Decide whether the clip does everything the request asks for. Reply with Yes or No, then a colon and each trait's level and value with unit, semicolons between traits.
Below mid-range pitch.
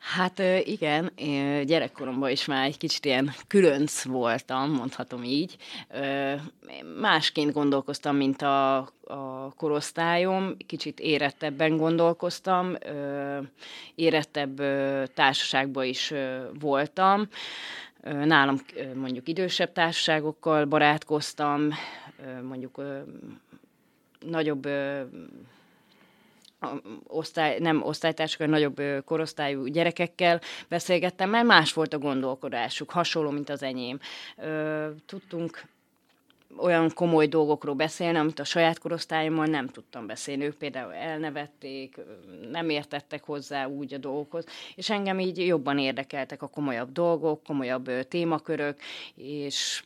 No: medium, 150 Hz